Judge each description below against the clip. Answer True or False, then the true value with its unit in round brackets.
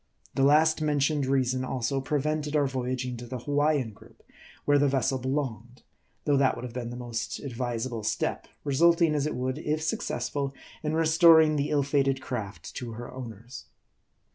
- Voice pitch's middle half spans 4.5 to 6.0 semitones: False (3.2 semitones)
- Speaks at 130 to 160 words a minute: False (170 wpm)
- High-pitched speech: False (135 Hz)